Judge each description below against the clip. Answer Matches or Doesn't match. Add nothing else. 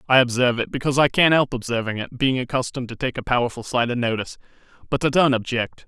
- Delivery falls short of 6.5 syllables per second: Doesn't match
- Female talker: Doesn't match